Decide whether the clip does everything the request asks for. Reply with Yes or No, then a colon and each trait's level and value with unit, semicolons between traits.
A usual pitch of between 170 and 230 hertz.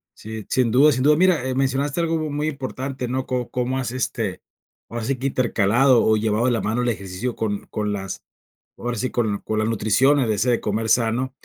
No: low, 120 Hz